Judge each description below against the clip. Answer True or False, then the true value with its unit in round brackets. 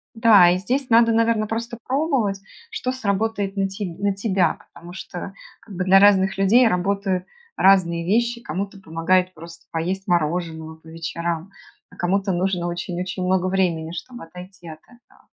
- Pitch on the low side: False (190 Hz)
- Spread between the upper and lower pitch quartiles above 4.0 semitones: False (3.4 semitones)